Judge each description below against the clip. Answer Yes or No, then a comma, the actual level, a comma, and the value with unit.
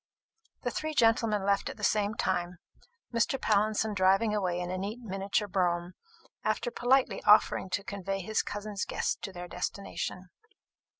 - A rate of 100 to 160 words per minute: Yes, average, 155 wpm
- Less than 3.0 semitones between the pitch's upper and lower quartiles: Yes, narrow, 2.6 semitones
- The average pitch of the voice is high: Yes, high, 200 Hz